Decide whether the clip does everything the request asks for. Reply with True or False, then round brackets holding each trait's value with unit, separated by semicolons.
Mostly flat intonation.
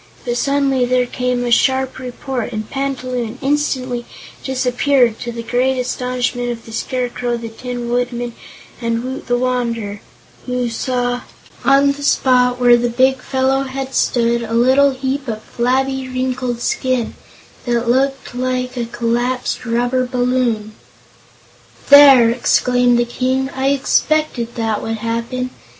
True (1.6 semitones)